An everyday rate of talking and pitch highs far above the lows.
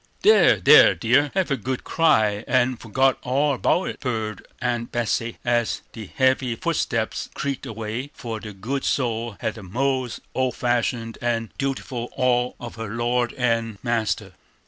No: average, 155 wpm; narrow, 2.4 semitones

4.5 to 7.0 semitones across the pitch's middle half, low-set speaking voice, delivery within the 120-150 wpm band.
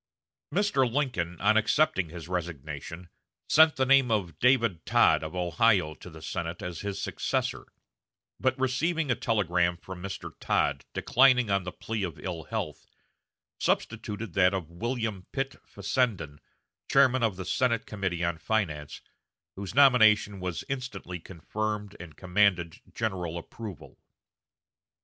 Yes: average, 5.3 semitones; low, 100 Hz; slow, 135 wpm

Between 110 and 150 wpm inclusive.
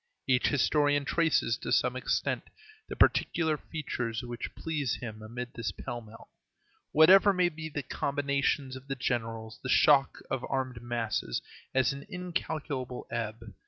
Yes: average, 145 wpm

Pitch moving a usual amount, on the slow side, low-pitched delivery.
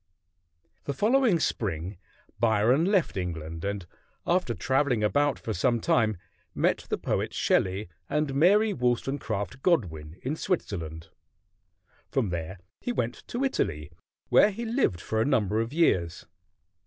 No: wide, 8.8 semitones; slow, 130 wpm; low, 115 Hz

